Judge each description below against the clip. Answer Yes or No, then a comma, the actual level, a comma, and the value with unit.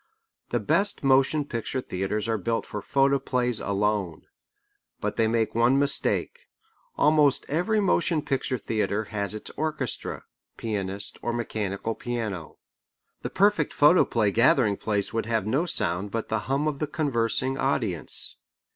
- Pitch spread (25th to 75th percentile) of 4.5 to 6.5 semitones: Yes, average, 4.8 semitones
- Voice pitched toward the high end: No, low, 115 Hz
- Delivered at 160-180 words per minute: No, average, 140 wpm